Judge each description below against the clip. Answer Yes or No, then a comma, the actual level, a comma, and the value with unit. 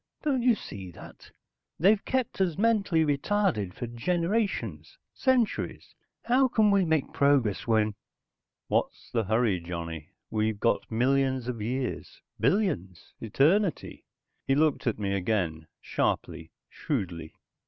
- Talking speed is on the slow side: Yes, slow, 120 wpm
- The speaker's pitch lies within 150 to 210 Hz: No, low, 130 Hz